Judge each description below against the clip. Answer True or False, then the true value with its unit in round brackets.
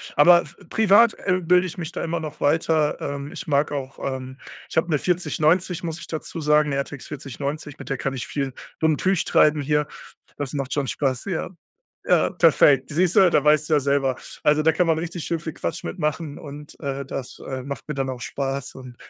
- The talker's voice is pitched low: False (150 Hz)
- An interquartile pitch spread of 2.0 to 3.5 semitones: True (3.0 semitones)